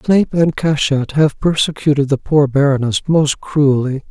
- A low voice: No, medium, 145 Hz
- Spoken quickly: No, average, 145 wpm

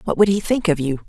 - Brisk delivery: Yes, fast, 335 wpm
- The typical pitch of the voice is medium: Yes, medium, 180 Hz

